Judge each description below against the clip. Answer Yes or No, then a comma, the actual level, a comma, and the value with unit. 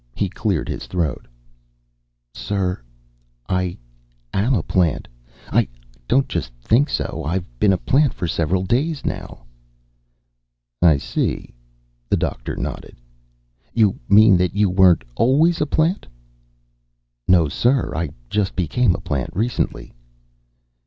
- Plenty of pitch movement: Yes, wide, 6.1 semitones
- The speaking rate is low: Yes, slow, 125 wpm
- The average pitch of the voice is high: No, very low, 95 Hz